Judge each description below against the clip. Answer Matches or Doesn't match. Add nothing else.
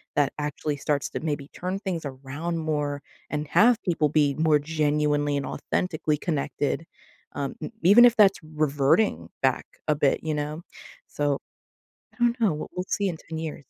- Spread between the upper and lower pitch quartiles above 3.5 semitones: Doesn't match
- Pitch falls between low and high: Matches